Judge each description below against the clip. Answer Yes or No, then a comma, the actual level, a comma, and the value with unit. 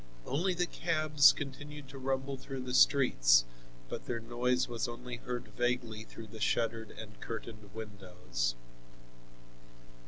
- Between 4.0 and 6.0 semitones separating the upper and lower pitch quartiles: No, average, 3.6 semitones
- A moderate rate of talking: No, slow, 130 wpm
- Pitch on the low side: Yes, low, 120 Hz